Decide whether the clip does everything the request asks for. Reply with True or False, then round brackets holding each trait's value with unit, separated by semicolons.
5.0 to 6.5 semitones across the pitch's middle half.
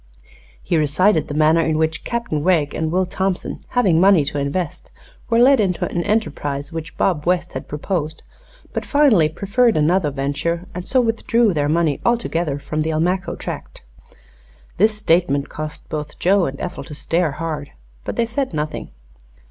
False (4.2 semitones)